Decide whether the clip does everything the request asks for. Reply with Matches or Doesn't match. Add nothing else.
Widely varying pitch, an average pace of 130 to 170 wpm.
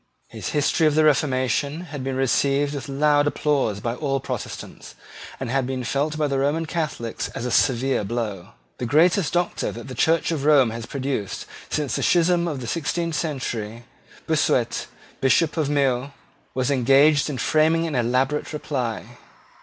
Doesn't match